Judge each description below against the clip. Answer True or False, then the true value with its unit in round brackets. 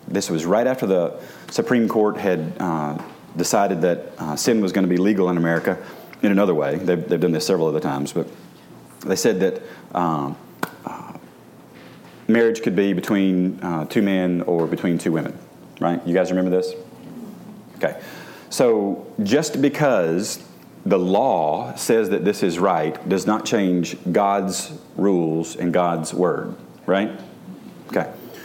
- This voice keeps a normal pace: True (155 wpm)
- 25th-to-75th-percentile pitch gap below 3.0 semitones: True (2.4 semitones)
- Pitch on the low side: True (90 Hz)